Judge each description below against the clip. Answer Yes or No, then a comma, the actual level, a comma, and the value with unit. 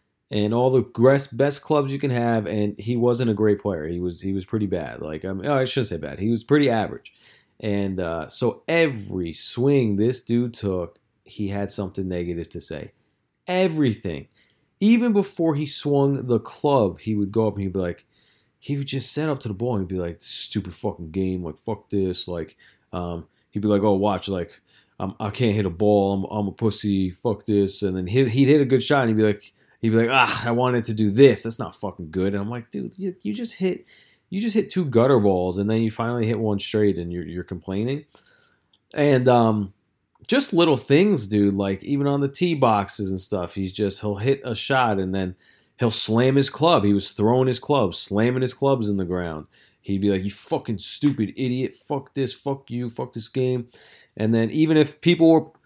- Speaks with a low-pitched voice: Yes, low, 110 Hz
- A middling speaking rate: No, fast, 220 wpm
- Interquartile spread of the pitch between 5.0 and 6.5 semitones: Yes, wide, 5.4 semitones